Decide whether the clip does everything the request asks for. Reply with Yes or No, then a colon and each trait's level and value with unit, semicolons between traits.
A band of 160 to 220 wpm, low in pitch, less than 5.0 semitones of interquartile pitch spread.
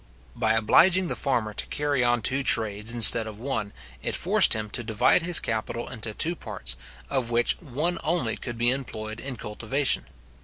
Yes: average, 180 wpm; low, 120 Hz; average, 4.2 semitones